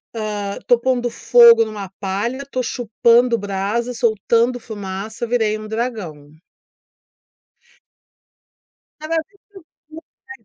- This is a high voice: Yes, high, 230 Hz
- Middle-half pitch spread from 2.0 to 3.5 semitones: Yes, average, 2.8 semitones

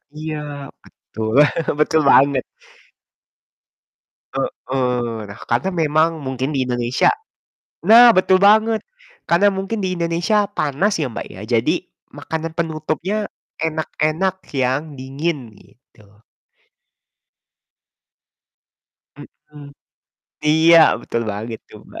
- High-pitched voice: No, medium, 155 Hz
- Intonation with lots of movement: Yes, wide, 6.0 semitones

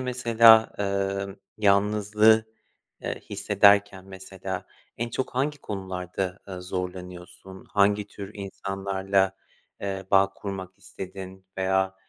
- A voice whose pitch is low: Yes, very low, 95 Hz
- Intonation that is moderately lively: No, narrow, 1.4 semitones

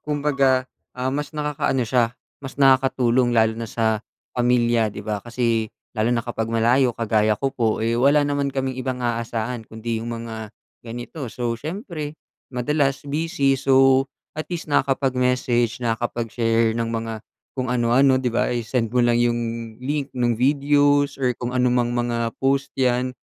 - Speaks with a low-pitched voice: Yes, low, 125 Hz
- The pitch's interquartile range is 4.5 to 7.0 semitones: No, narrow, 2.6 semitones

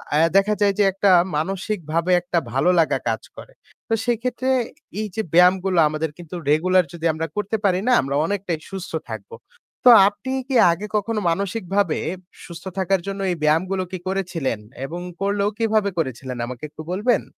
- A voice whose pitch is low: No, medium, 185 Hz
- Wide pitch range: No, average, 3.7 semitones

